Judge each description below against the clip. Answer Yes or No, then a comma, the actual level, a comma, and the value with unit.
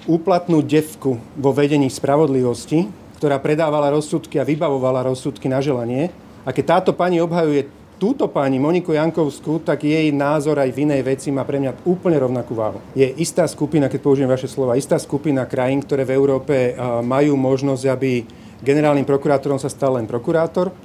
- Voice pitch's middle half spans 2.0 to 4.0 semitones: Yes, average, 2.8 semitones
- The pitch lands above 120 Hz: Yes, medium, 140 Hz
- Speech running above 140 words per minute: Yes, fast, 165 wpm